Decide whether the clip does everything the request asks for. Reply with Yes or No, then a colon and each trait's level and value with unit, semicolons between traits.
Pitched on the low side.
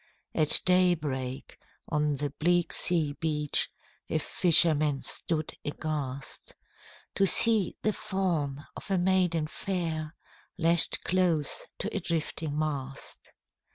No: medium, 160 Hz